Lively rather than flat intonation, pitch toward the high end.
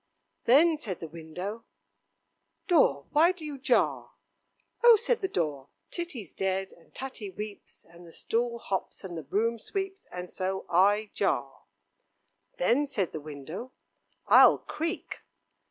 Yes: wide, 9.0 semitones; high, 205 Hz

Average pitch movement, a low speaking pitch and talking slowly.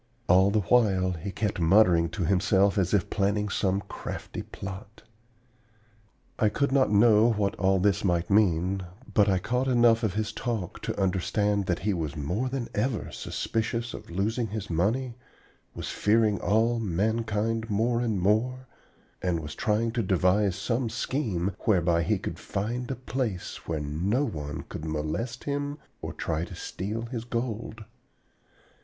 No: average, 3.8 semitones; low, 105 Hz; average, 160 wpm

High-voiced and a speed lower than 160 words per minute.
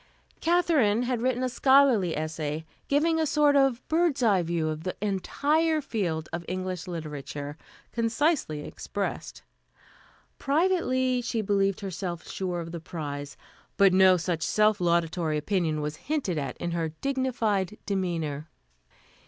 Yes: high, 195 Hz; slow, 135 wpm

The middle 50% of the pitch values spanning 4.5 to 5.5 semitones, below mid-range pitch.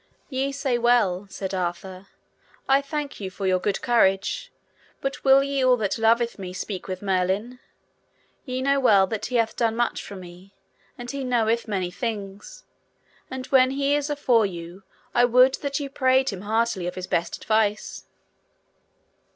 No: average, 5.2 semitones; high, 230 Hz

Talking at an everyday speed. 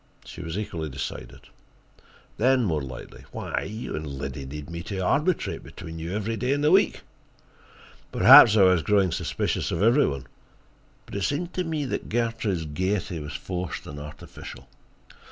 Yes: average, 165 wpm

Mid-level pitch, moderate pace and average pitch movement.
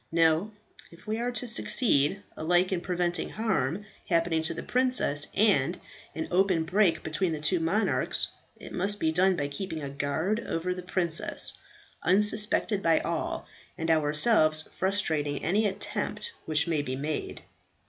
Yes: medium, 175 Hz; average, 150 wpm; average, 4.3 semitones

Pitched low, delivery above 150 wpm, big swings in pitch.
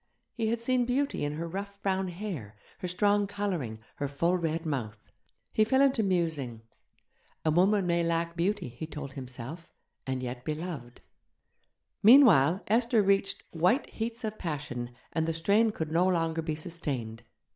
No: medium, 170 Hz; average, 160 wpm; wide, 5.7 semitones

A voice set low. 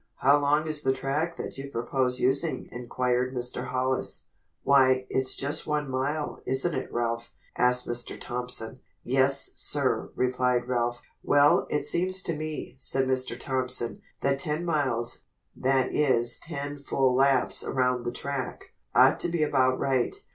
Yes: low, 130 Hz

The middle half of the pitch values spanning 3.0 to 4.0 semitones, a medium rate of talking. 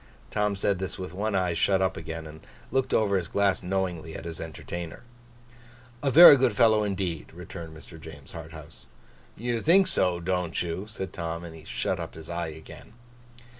Yes: average, 3.6 semitones; average, 175 wpm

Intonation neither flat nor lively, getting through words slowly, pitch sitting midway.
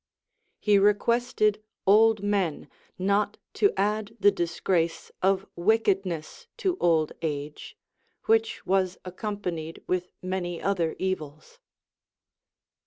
No: average, 3.3 semitones; slow, 100 wpm; high, 195 Hz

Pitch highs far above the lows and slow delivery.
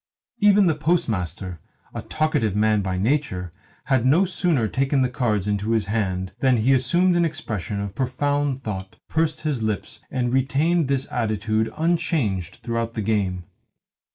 No: wide, 6.1 semitones; average, 155 wpm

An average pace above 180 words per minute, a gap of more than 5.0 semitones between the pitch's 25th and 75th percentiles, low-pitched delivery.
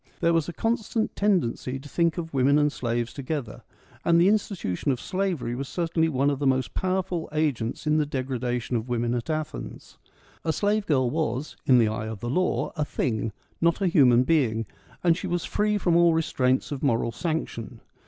No: average, 195 wpm; wide, 5.4 semitones; medium, 145 Hz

